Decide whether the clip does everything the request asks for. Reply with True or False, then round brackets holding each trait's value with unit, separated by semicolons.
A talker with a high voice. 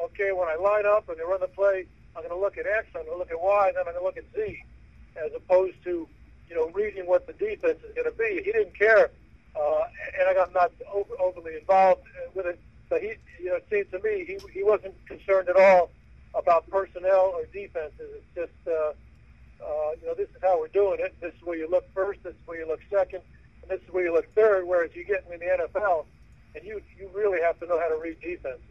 True (195 Hz)